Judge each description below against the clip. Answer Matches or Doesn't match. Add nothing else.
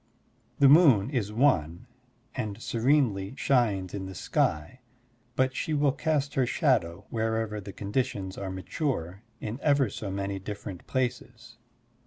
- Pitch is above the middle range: Doesn't match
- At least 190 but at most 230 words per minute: Doesn't match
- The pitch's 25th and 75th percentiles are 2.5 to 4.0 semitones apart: Doesn't match